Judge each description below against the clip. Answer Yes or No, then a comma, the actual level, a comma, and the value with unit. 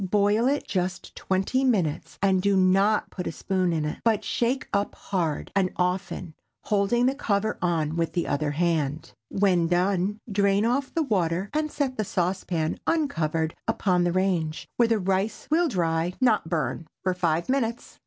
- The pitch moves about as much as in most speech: Yes, average, 4.1 semitones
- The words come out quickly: No, average, 170 wpm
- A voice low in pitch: No, high, 190 Hz